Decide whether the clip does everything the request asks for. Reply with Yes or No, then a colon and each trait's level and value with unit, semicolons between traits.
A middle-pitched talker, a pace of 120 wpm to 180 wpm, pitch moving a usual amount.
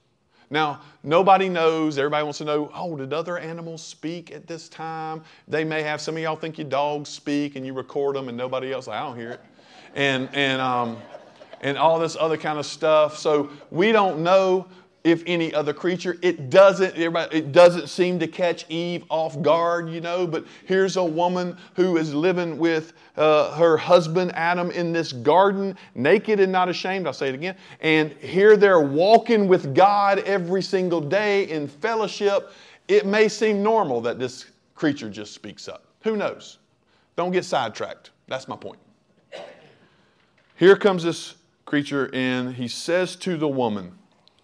Yes: medium, 165 Hz; average, 175 wpm; average, 3.5 semitones